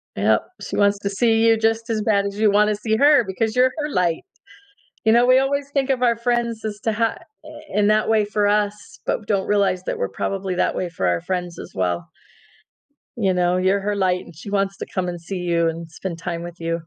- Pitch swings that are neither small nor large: Yes, average, 3.8 semitones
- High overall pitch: Yes, high, 200 Hz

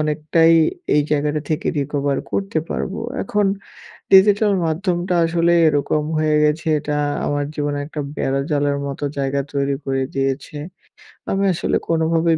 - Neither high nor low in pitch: Yes, medium, 150 Hz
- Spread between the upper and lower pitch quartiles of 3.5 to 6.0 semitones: No, average, 2.7 semitones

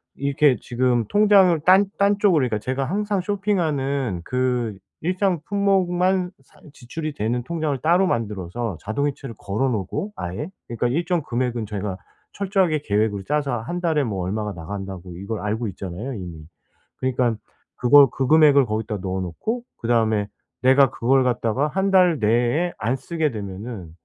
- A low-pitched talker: Yes, low, 130 Hz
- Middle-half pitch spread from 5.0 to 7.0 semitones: No, wide, 7.6 semitones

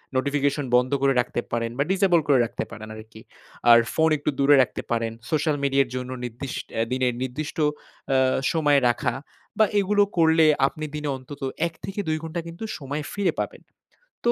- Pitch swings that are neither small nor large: Yes, average, 4.0 semitones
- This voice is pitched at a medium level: Yes, medium, 145 Hz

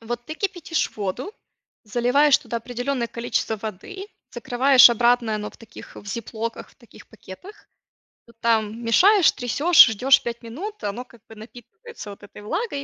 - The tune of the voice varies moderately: Yes, average, 4.1 semitones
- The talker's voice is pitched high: Yes, high, 240 Hz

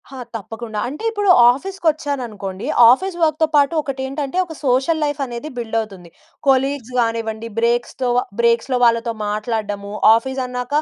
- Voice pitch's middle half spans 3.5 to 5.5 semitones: Yes, average, 3.8 semitones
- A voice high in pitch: Yes, very high, 250 Hz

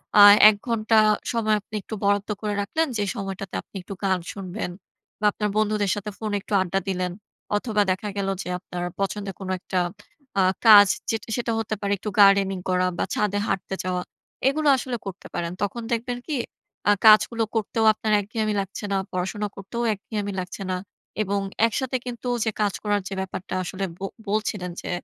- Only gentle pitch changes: Yes, narrow, 2.1 semitones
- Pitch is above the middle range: Yes, high, 205 Hz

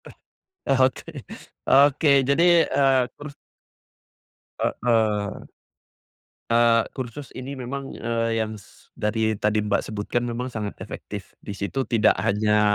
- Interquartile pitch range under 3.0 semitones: No, average, 3.6 semitones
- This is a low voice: Yes, low, 115 Hz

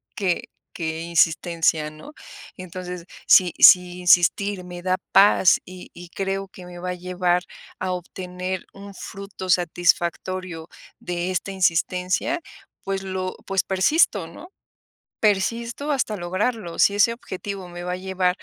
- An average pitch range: No, narrow, 1.8 semitones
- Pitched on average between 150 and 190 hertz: Yes, medium, 185 Hz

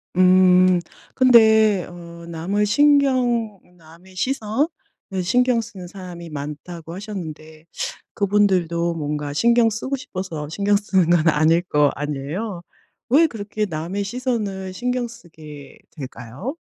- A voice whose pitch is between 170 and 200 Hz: Yes, medium, 185 Hz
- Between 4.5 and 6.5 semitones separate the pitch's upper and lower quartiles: Yes, average, 5.1 semitones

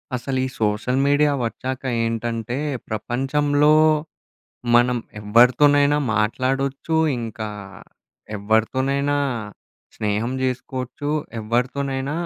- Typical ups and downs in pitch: Yes, average, 3.4 semitones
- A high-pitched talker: No, low, 130 Hz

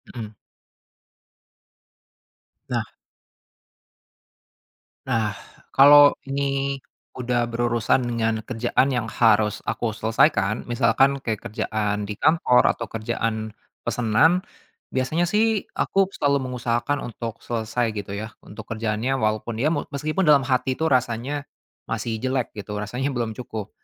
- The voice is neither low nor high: No, low, 120 Hz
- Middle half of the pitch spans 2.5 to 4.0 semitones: Yes, average, 3.7 semitones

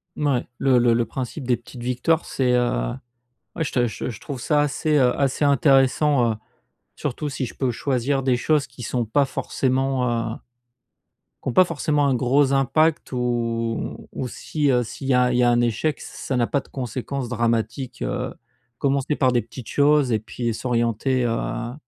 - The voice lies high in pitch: No, low, 125 Hz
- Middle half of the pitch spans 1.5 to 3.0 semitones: Yes, average, 2.7 semitones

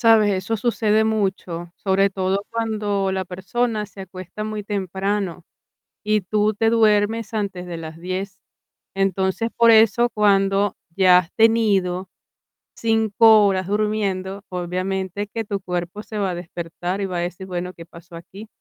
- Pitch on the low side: No, high, 195 Hz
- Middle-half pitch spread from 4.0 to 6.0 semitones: No, narrow, 2.6 semitones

